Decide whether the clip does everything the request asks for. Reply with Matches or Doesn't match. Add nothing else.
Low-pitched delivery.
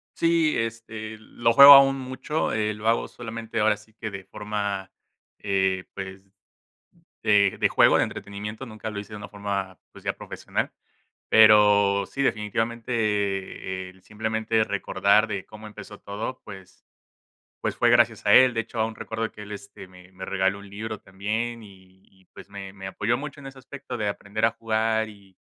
Matches